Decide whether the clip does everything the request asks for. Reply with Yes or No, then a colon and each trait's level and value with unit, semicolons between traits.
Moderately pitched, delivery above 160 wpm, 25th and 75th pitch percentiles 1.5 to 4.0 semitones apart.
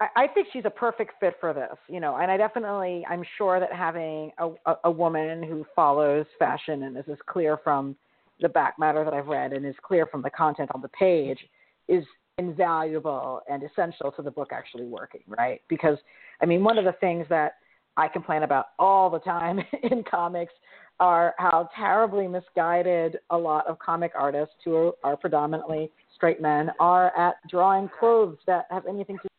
Yes: medium, 170 Hz; average, 185 wpm; average, 3.2 semitones